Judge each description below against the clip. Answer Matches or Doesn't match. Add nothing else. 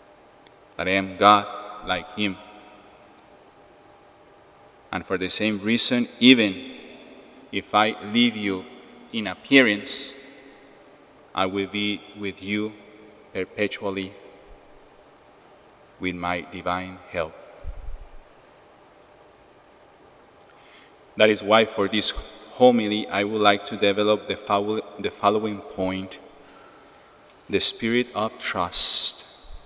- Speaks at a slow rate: Matches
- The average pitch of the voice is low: Matches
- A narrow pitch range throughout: Matches